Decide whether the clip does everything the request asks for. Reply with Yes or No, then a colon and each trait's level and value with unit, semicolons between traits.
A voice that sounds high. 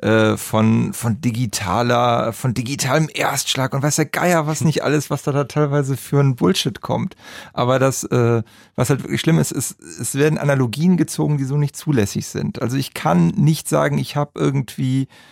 No: low, 135 Hz